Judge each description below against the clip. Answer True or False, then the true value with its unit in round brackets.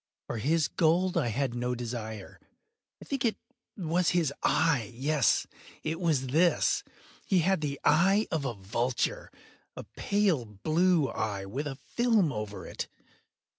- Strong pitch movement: True (6.5 semitones)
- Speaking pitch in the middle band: True (150 Hz)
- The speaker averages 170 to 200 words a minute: False (140 wpm)